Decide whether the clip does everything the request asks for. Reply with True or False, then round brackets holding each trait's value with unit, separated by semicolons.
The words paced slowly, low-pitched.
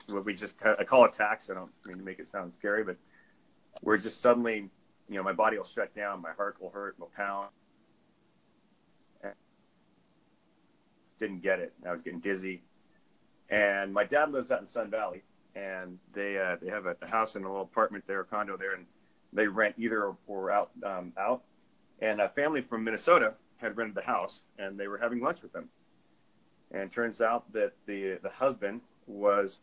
False (190 wpm; 100 Hz)